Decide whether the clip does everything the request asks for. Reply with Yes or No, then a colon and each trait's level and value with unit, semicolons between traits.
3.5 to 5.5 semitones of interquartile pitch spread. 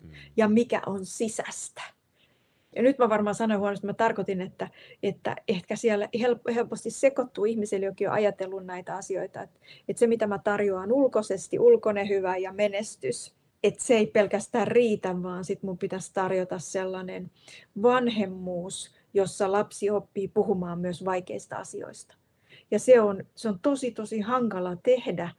No: average, 3.0 semitones